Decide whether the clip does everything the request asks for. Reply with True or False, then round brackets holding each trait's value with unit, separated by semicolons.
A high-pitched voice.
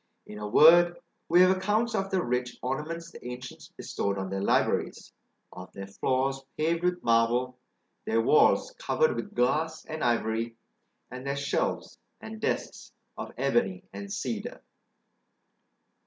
False (130 Hz)